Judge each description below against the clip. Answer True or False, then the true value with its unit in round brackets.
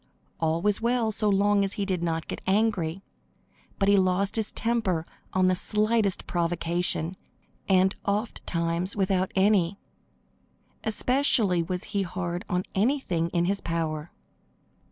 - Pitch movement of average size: True (3.2 semitones)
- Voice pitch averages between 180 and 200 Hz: True (190 Hz)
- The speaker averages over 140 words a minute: False (135 wpm)